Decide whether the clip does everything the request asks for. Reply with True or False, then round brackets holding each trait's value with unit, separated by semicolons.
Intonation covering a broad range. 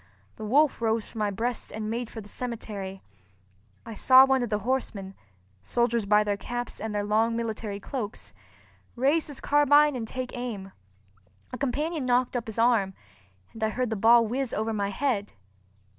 False (3.2 semitones)